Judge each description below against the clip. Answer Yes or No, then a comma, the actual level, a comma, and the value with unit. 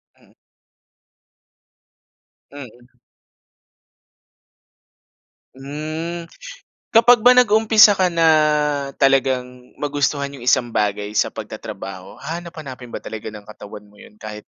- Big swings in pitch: Yes, wide, 6.2 semitones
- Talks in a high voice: No, medium, 140 Hz